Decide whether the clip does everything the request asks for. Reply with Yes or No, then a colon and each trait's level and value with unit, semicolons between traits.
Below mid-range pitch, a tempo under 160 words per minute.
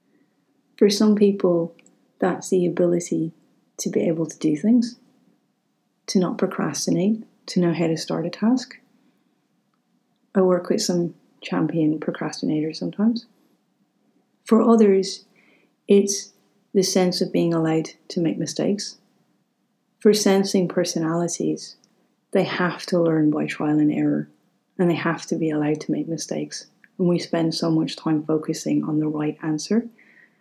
No: medium, 180 Hz; average, 140 wpm